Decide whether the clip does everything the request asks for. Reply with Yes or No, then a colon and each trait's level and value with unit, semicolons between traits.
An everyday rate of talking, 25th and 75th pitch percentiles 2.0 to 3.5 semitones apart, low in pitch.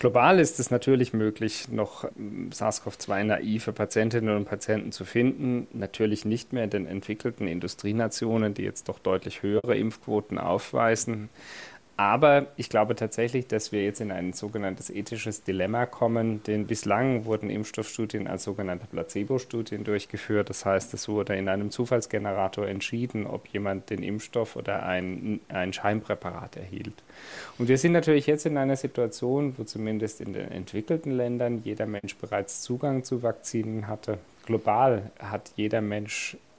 Yes: average, 150 wpm; average, 2.8 semitones; low, 110 Hz